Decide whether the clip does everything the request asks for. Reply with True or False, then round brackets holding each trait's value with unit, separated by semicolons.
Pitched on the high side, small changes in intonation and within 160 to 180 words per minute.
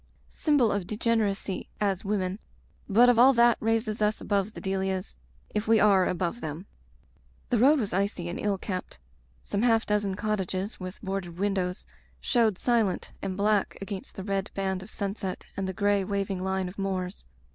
True (200 Hz; 2.2 semitones; 170 wpm)